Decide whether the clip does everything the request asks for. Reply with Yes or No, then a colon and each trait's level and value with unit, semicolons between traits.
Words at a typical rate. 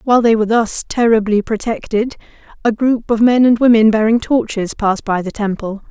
Yes: average, 185 wpm